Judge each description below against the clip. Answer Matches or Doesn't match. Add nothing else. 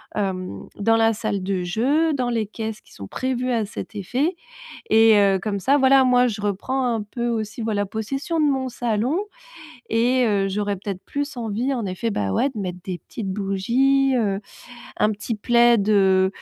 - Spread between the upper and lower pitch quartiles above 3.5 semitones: Matches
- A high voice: Matches